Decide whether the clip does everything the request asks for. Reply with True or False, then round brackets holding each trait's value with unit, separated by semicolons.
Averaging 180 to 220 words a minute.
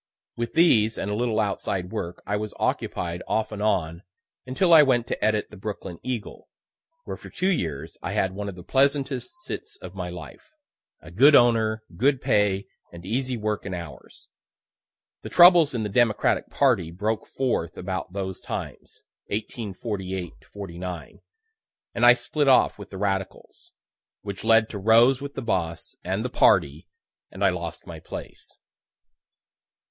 False (160 wpm)